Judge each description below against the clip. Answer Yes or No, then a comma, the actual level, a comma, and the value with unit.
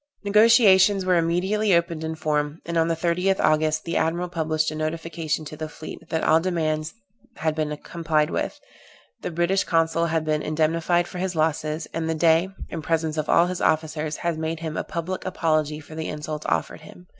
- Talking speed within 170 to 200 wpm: Yes, average, 190 wpm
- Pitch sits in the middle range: Yes, medium, 160 Hz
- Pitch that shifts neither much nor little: No, narrow, 1.8 semitones